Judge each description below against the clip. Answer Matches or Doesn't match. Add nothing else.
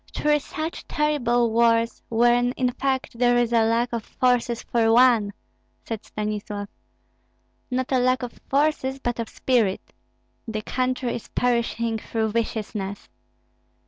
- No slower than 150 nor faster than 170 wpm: Doesn't match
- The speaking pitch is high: Matches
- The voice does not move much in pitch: Matches